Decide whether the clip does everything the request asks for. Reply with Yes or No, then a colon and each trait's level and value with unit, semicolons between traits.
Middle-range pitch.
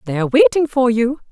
No: high, 240 Hz